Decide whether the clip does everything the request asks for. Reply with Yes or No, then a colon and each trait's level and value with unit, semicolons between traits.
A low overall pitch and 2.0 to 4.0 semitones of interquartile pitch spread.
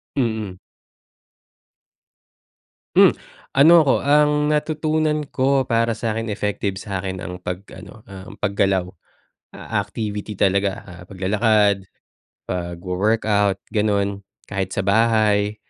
Yes: low, 105 Hz; average, 3.0 semitones